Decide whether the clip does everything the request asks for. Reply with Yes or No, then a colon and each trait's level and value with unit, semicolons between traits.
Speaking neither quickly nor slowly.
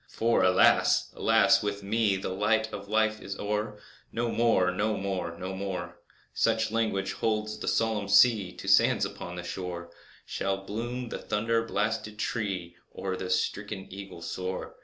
Yes: average, 155 wpm